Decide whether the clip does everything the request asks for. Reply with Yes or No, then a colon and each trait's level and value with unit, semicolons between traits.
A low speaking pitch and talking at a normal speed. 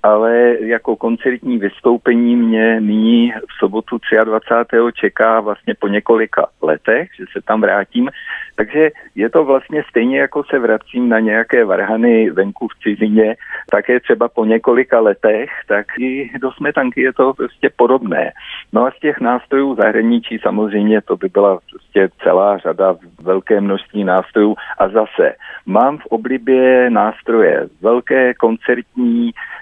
Yes: low, 115 Hz; average, 140 wpm